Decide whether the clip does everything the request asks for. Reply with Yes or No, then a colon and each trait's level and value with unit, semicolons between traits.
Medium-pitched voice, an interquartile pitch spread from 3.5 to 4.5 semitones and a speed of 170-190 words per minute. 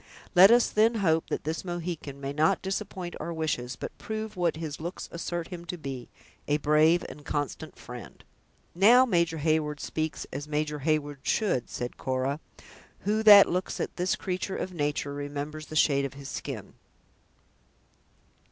No: medium, 160 Hz; average, 3.9 semitones; average, 160 wpm